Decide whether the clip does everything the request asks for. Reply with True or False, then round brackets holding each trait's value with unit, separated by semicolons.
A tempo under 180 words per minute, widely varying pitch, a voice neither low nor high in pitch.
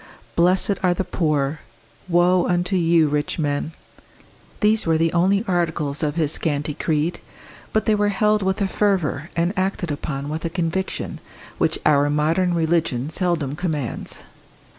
False (150 wpm; 3.5 semitones; 170 Hz)